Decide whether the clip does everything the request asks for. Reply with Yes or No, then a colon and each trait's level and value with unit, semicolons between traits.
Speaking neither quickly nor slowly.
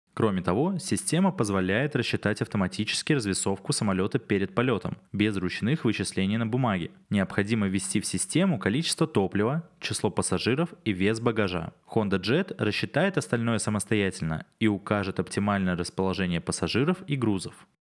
Yes: average, 130 wpm